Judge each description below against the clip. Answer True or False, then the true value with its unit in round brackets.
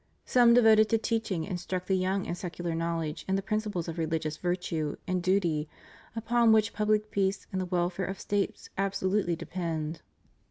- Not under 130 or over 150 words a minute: False (165 wpm)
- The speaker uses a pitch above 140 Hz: True (185 Hz)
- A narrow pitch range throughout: False (3.8 semitones)